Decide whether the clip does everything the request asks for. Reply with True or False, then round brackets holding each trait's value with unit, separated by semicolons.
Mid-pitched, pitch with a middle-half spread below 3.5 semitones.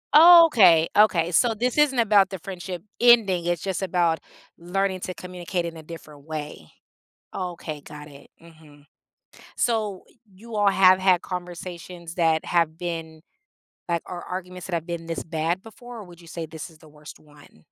True (175 Hz; 3.0 semitones)